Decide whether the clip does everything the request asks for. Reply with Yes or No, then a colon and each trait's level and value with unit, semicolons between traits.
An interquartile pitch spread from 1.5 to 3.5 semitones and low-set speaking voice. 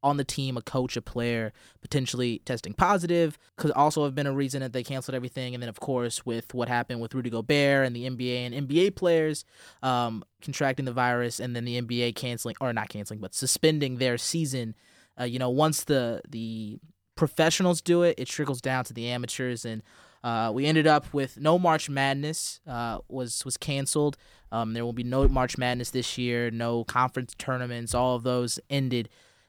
Yes: average, 2.9 semitones; low, 125 Hz